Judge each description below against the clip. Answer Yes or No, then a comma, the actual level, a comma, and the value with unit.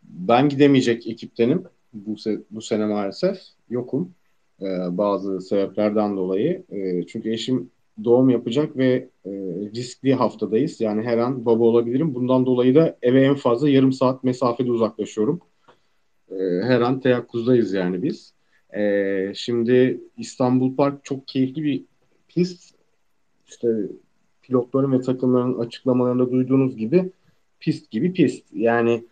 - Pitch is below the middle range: Yes, low, 125 Hz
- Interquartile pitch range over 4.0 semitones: No, average, 3.5 semitones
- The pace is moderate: Yes, average, 130 wpm